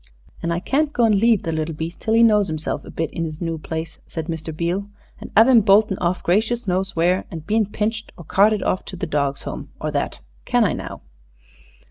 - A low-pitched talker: No, medium, 185 Hz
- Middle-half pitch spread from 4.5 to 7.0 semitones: Yes, average, 4.8 semitones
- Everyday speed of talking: No, fast, 225 wpm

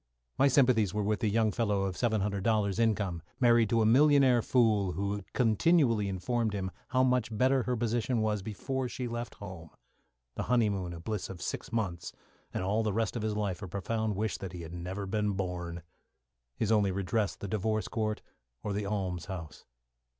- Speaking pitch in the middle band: No, low, 105 Hz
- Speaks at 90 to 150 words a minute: No, average, 185 wpm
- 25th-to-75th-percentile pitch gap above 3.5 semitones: No, average, 3.1 semitones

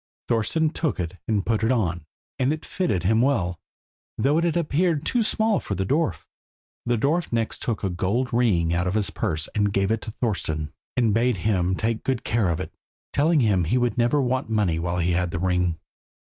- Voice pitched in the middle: No, low, 110 Hz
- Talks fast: Yes, fast, 210 wpm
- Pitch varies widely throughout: Yes, wide, 6.3 semitones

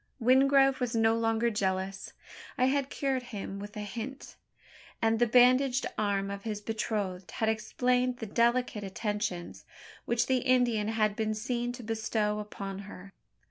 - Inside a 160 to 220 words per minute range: No, average, 150 wpm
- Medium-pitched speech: No, high, 225 Hz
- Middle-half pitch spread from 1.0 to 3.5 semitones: Yes, average, 3.2 semitones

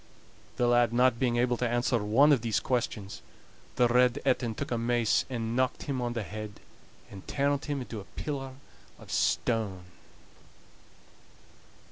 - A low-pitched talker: Yes, low, 120 Hz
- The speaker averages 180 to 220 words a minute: No, average, 155 wpm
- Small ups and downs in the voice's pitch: Yes, narrow, 2.1 semitones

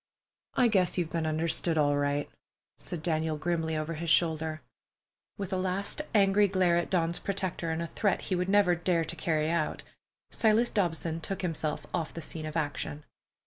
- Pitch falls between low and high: Yes, medium, 170 Hz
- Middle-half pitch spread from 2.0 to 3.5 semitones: Yes, average, 2.9 semitones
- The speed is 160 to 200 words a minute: Yes, average, 180 wpm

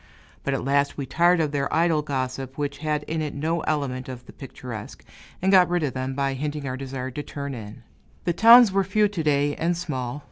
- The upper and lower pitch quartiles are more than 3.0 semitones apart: Yes, average, 3.7 semitones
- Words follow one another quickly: Yes, fast, 220 wpm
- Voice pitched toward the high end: No, medium, 145 Hz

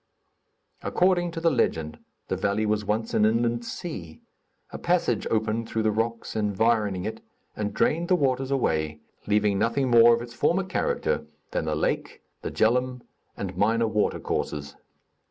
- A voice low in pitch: Yes, low, 115 Hz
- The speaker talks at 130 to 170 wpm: Yes, average, 155 wpm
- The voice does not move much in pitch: No, average, 3.8 semitones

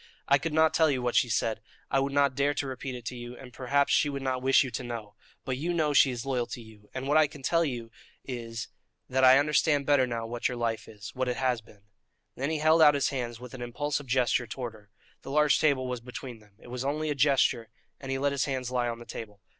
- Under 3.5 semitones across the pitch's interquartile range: Yes, average, 2.9 semitones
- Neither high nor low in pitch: No, low, 130 Hz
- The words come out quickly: Yes, fast, 265 wpm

